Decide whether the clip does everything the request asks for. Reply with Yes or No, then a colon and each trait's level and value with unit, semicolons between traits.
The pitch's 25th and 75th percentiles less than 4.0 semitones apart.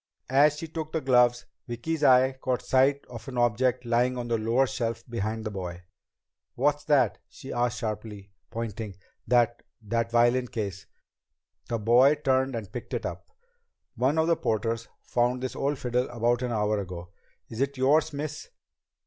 Yes: average, 2.7 semitones